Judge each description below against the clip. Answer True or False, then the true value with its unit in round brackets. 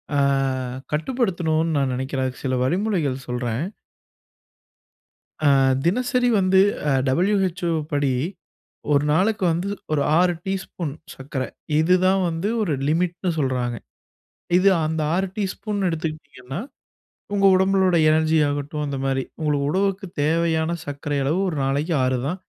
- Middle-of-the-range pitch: True (160 Hz)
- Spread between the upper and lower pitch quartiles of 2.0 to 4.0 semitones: False (4.8 semitones)